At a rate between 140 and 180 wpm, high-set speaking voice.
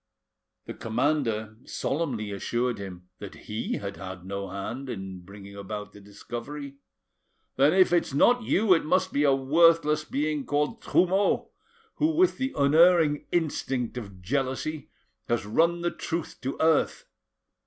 No: average, 145 wpm; medium, 140 Hz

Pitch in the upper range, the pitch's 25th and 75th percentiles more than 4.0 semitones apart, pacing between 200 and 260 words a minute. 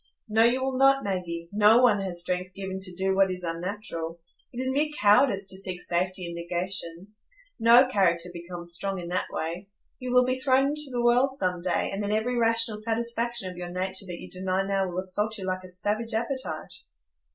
Yes: high, 195 Hz; average, 4.5 semitones; fast, 205 wpm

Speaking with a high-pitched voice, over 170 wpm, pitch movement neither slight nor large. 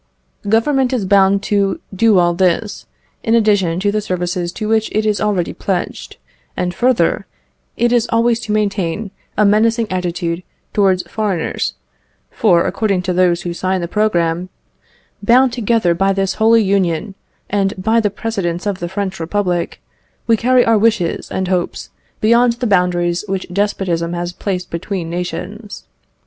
No: high, 195 Hz; average, 155 wpm; average, 3.5 semitones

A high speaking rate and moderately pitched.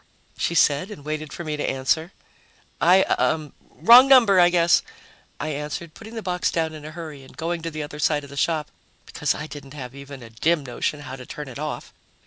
Yes: fast, 220 wpm; medium, 155 Hz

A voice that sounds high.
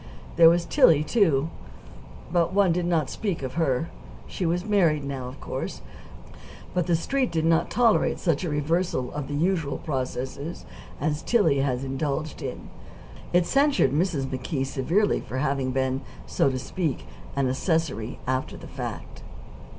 No: medium, 155 Hz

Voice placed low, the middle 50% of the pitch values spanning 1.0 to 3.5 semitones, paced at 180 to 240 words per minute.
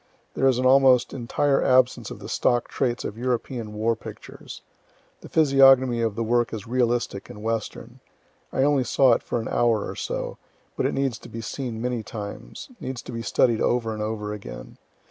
Yes: low, 120 Hz; narrow, 2.5 semitones; average, 190 wpm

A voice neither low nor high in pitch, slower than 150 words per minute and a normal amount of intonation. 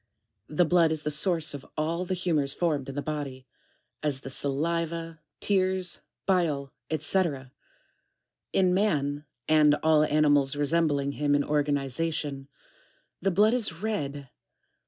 Yes: medium, 155 Hz; slow, 135 wpm; average, 3.0 semitones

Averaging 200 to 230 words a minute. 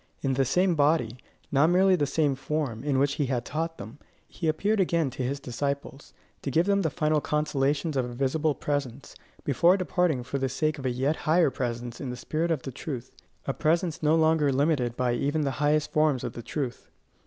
Yes: fast, 205 wpm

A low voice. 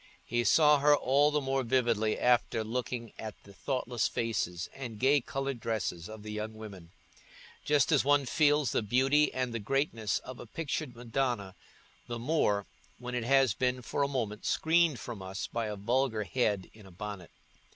Yes: low, 120 Hz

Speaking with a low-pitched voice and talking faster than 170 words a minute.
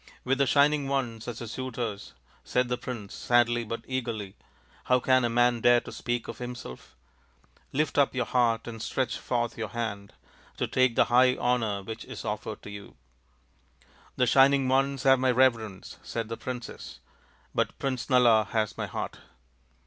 Yes: low, 120 Hz; average, 180 wpm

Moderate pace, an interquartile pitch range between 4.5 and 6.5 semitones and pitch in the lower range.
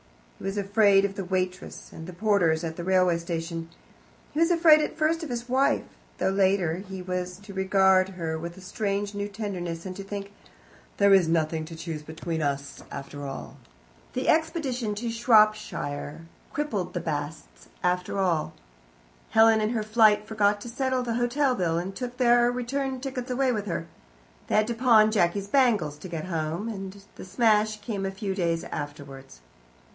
No: average, 175 wpm; average, 5.1 semitones; high, 195 Hz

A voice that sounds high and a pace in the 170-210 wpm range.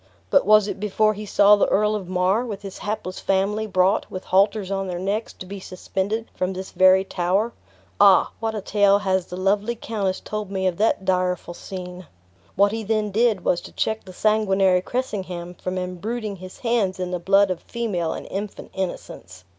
Yes: high, 195 Hz; average, 195 wpm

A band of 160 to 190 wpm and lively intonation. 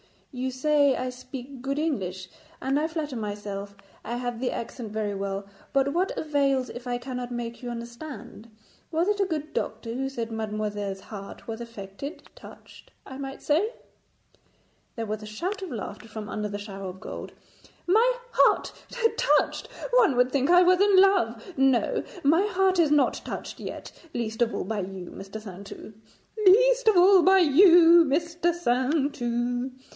Yes: average, 165 wpm; wide, 6.9 semitones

